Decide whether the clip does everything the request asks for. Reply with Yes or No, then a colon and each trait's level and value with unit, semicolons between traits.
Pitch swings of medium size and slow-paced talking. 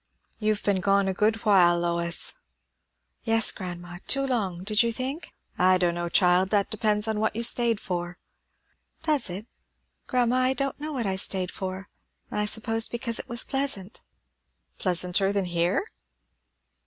No: average, 4.2 semitones; average, 155 wpm